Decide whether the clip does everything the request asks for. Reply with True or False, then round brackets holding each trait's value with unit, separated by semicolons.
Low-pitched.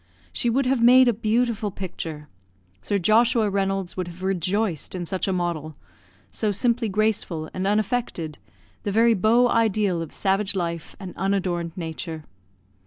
False (195 Hz)